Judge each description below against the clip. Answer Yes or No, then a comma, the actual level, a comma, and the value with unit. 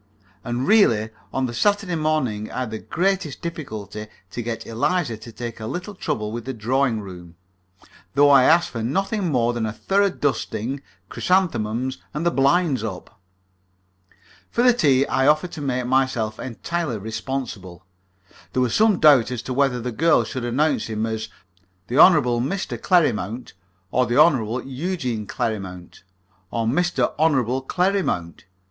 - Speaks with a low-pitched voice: Yes, low, 130 Hz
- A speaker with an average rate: Yes, average, 155 wpm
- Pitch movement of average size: No, wide, 6.0 semitones